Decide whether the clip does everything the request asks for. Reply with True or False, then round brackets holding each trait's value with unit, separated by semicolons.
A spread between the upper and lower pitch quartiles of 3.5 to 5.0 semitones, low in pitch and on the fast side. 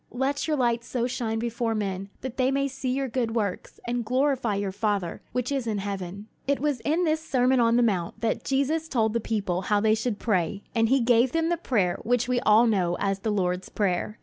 False (4.2 semitones; 230 Hz; 225 wpm)